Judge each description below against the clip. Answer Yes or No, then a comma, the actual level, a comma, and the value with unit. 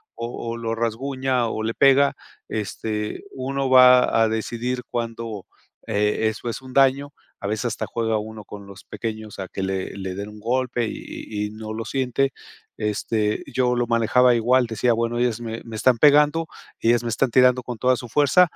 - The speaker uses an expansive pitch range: No, average, 2.7 semitones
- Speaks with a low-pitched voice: Yes, low, 115 Hz